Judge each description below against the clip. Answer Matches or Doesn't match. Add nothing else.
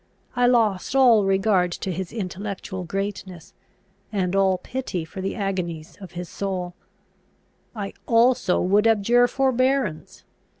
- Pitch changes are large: Doesn't match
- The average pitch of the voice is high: Matches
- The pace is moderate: Doesn't match